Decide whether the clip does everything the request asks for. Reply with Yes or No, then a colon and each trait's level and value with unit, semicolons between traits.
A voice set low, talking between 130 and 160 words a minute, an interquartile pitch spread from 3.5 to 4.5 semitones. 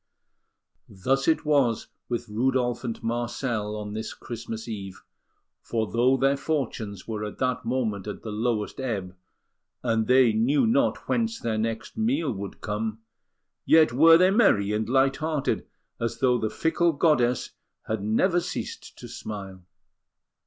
Yes: low, 120 Hz; average, 145 wpm; average, 4.1 semitones